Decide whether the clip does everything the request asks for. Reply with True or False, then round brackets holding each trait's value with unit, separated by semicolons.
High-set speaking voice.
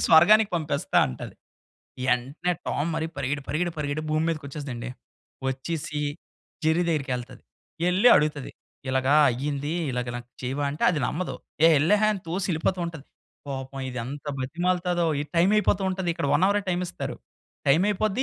False (155 Hz)